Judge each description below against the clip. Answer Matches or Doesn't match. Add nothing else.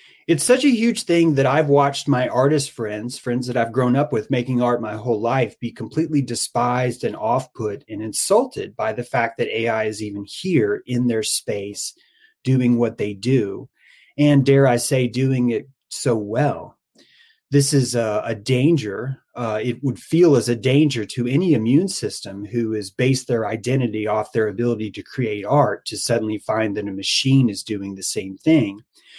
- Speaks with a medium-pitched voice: Doesn't match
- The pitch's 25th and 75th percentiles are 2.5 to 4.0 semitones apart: Doesn't match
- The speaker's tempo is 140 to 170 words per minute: Doesn't match